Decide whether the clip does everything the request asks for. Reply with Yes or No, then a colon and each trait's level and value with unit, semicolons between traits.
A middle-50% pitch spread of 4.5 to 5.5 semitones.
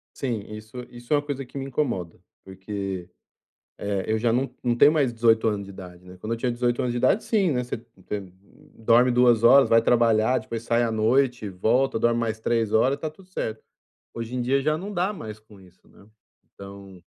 No: average, 3.2 semitones